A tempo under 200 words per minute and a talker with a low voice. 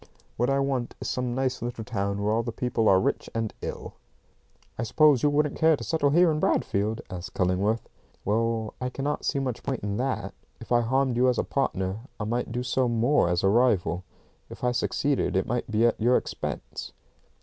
No: fast, 205 wpm; low, 120 Hz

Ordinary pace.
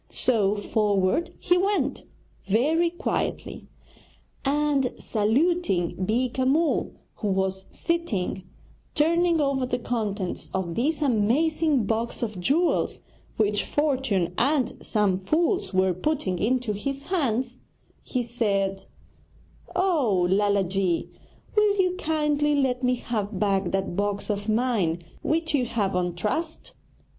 No: slow, 120 wpm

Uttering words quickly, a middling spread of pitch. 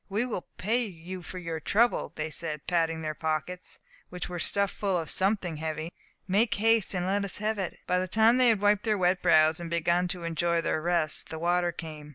Yes: fast, 215 wpm; average, 3.5 semitones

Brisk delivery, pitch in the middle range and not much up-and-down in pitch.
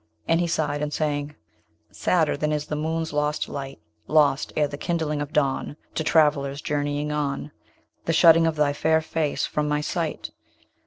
No: average, 170 wpm; medium, 150 Hz; narrow, 1.6 semitones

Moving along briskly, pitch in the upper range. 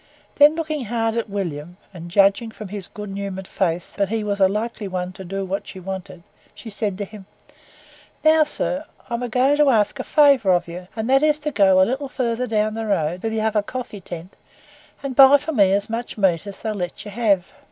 Yes: fast, 220 wpm; high, 210 Hz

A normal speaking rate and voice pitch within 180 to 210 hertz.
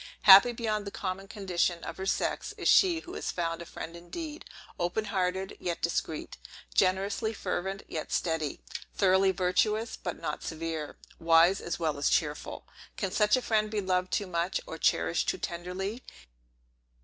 Yes: average, 160 wpm; high, 190 Hz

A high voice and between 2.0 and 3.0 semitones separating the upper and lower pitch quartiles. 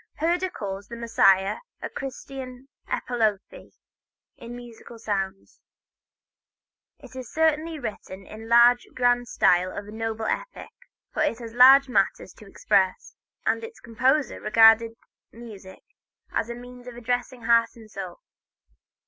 Yes: high, 235 Hz; average, 2.7 semitones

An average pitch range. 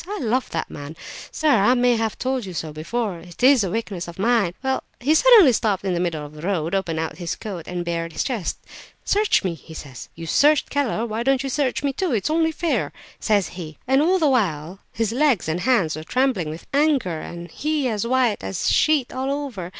No: wide, 7.6 semitones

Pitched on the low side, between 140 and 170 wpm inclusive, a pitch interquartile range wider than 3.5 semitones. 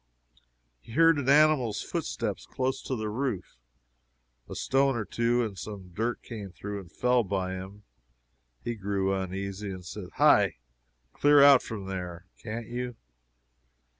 Yes: low, 110 Hz; average, 145 wpm; average, 4.6 semitones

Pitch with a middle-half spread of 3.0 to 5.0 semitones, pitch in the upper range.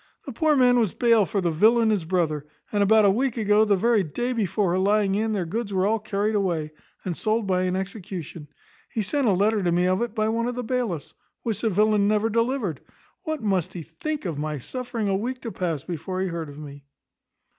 Yes: average, 4.0 semitones; high, 205 Hz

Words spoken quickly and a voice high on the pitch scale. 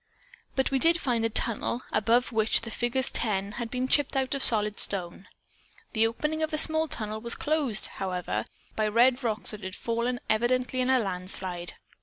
No: average, 185 wpm; high, 235 Hz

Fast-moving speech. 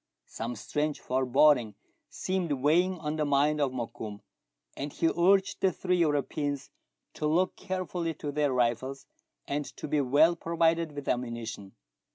No: average, 150 wpm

